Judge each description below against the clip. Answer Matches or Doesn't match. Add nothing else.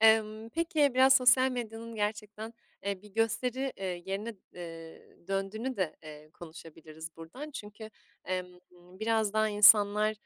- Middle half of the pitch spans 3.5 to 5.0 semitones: Matches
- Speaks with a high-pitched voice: Matches